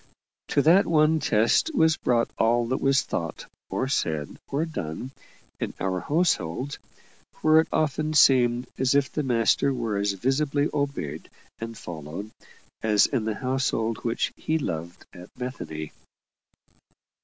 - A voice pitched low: Yes, low, 125 Hz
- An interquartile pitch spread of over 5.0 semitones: Yes, wide, 5.4 semitones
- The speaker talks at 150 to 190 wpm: No, average, 140 wpm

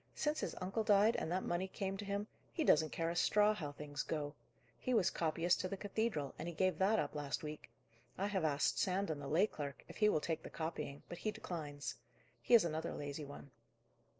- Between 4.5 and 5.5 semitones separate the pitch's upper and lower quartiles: Yes, average, 5.1 semitones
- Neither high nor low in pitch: Yes, medium, 175 Hz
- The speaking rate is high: Yes, fast, 220 wpm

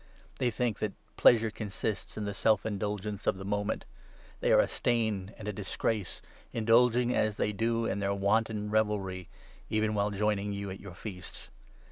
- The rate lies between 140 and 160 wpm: No, average, 175 wpm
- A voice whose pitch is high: No, low, 105 Hz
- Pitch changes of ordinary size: No, narrow, 1.7 semitones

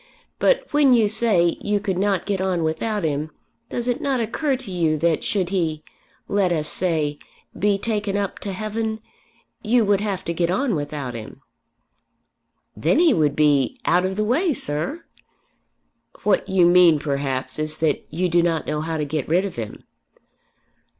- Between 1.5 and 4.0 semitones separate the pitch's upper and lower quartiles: No, average, 5.3 semitones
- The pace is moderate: Yes, average, 175 wpm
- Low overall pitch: No, medium, 180 Hz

